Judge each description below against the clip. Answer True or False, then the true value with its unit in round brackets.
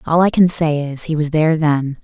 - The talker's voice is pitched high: False (155 Hz)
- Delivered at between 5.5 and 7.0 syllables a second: False (5.3 syllables/s)